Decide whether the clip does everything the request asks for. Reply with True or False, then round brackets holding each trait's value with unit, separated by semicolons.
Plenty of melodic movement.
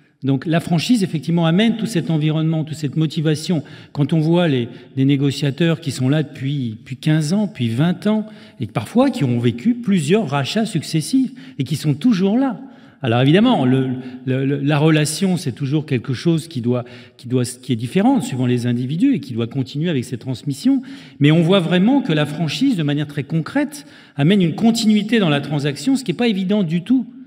True (6.9 semitones)